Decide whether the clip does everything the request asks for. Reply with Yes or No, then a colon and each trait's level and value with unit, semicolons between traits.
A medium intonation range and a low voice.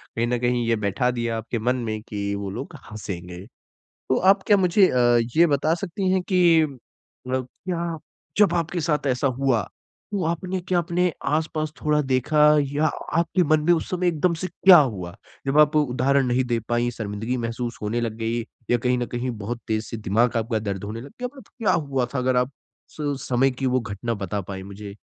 No: wide, 5.8 semitones; low, 125 Hz